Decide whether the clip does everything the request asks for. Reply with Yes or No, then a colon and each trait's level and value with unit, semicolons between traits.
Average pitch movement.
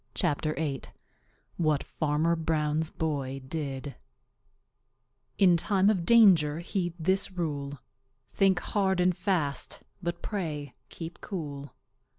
Yes: average, 3.8 semitones